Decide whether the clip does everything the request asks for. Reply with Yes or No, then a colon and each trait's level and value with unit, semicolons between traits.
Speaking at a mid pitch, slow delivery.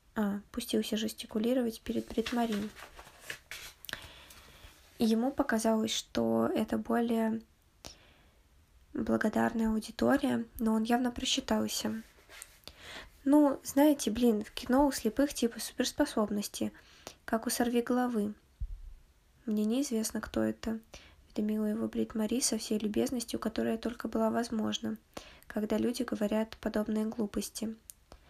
No: high, 220 Hz; slow, 105 wpm